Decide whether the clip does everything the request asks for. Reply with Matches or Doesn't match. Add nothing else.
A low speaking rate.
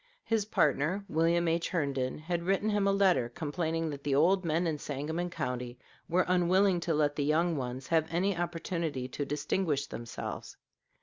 Doesn't match